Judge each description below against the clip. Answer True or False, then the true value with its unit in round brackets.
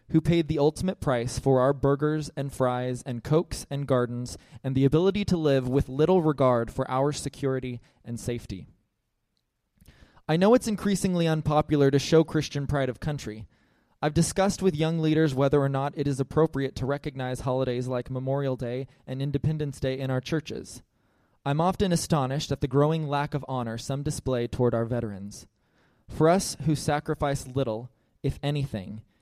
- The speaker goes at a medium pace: True (170 wpm)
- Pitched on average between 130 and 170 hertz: True (140 Hz)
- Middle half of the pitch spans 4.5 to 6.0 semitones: False (3.5 semitones)